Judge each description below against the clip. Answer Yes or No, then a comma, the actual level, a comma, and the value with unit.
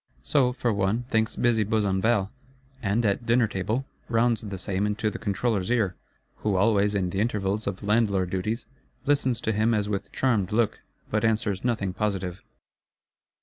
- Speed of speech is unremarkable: Yes, average, 155 wpm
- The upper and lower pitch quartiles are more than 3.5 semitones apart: No, average, 2.9 semitones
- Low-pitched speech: Yes, low, 105 Hz